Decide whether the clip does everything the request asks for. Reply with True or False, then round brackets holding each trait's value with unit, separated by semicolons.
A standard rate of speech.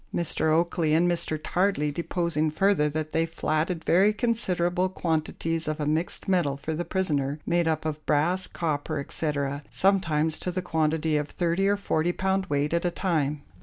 True (170 wpm)